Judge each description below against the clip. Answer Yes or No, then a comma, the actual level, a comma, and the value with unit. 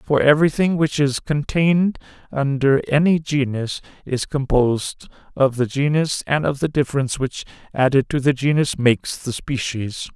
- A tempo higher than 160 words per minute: No, average, 150 wpm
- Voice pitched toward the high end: No, medium, 140 Hz